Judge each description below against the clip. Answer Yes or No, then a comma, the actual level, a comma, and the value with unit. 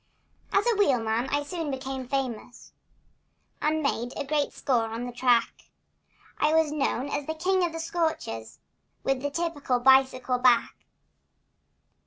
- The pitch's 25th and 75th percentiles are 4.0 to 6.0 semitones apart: Yes, average, 4.3 semitones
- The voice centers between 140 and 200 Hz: No, very high, 270 Hz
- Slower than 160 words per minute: Yes, average, 145 wpm